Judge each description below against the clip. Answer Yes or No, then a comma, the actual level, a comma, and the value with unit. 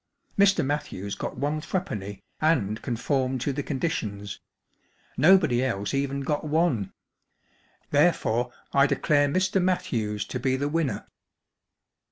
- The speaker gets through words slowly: Yes, slow, 125 wpm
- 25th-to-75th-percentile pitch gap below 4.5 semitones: No, average, 5.2 semitones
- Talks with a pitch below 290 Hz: Yes, medium, 140 Hz